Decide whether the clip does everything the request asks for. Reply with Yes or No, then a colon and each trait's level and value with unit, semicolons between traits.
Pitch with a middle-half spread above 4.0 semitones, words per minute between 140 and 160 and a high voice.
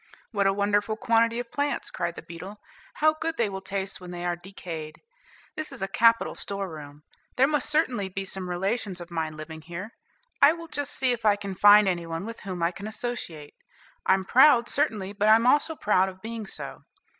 No: average, 4.5 semitones; fast, 205 wpm; high, 200 Hz